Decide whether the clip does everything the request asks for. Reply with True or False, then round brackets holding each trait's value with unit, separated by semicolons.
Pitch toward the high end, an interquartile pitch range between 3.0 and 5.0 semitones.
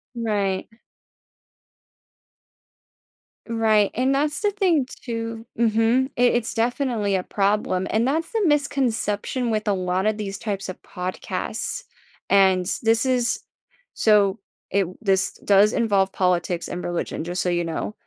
True (215 Hz; 4.0 semitones)